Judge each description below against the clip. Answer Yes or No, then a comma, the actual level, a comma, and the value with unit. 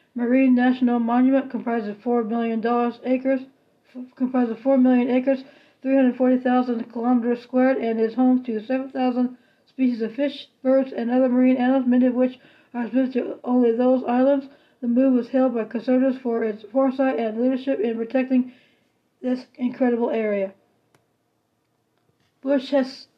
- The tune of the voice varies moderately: No, narrow, 1.6 semitones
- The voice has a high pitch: Yes, very high, 255 Hz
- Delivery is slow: No, average, 150 wpm